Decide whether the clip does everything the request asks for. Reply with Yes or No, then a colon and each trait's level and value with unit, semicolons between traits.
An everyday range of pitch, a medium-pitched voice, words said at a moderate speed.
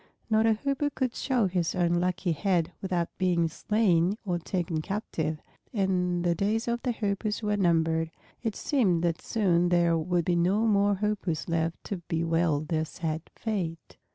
Yes: average, 3.9 semitones; medium, 180 Hz; average, 160 wpm